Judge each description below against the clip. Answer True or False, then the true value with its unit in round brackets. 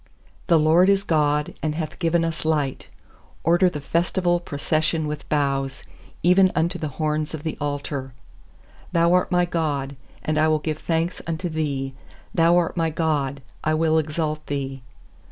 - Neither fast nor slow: True (160 wpm)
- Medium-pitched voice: True (155 Hz)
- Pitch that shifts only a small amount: True (2.3 semitones)